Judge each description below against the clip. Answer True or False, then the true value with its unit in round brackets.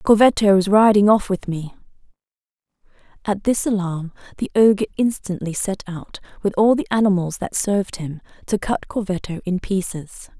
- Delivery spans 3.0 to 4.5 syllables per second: False (5.1 syllables/s)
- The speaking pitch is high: True (195 Hz)